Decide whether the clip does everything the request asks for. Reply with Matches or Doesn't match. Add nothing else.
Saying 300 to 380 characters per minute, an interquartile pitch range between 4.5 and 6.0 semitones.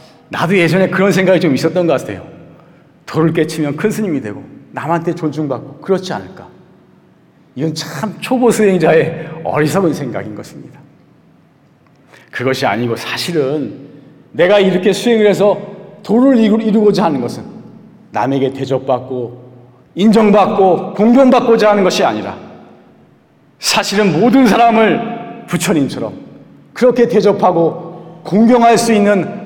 Doesn't match